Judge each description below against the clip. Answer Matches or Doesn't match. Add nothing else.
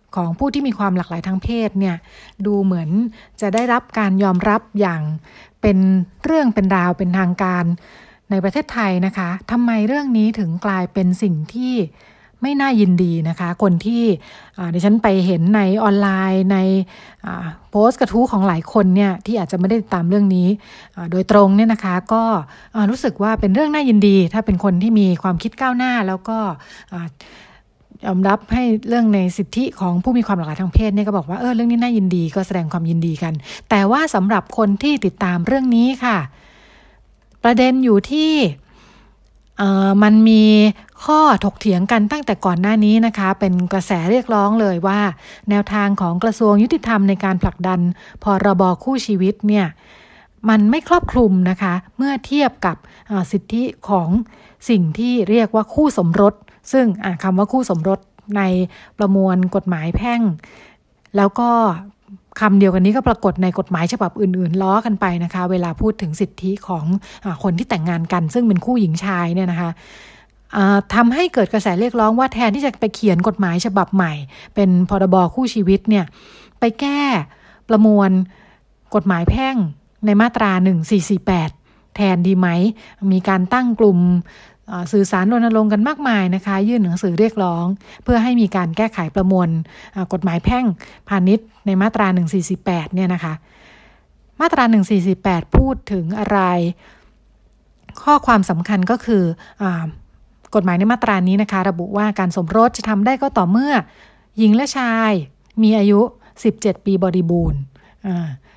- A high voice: Matches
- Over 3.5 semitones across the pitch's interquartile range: Doesn't match